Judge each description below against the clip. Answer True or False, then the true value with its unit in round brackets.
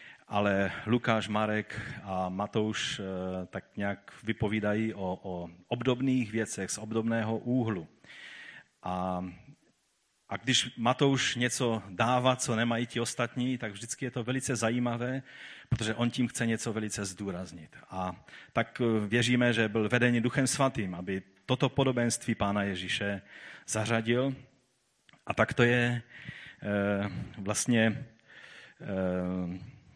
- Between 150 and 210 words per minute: False (120 wpm)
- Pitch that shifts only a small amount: False (3.5 semitones)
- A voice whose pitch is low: True (110 Hz)